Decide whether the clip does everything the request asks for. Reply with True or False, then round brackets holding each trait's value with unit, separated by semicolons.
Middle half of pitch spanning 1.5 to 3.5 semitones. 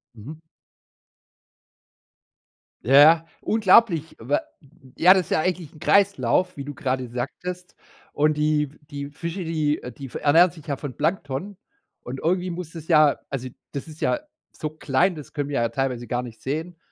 False (4.2 semitones)